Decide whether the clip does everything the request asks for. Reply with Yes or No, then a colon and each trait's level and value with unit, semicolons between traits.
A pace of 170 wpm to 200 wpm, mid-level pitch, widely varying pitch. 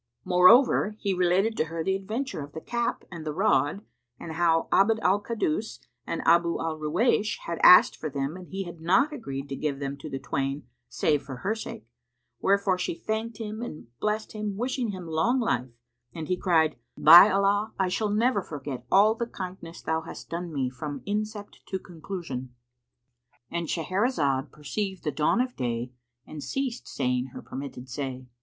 Yes: average, 175 wpm; medium, 170 Hz; wide, 6.5 semitones